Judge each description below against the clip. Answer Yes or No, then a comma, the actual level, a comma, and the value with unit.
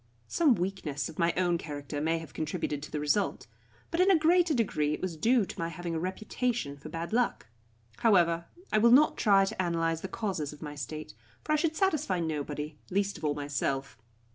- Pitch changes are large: Yes, wide, 6.5 semitones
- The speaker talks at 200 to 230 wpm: Yes, fast, 205 wpm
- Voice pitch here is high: No, medium, 170 Hz